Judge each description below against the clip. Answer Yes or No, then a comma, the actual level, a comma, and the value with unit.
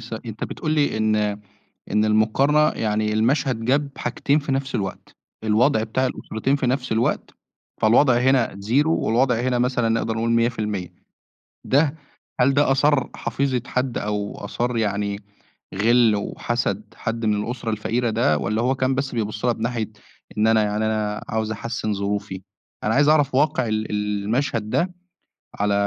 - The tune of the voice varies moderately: Yes, average, 3.5 semitones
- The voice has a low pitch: Yes, low, 115 Hz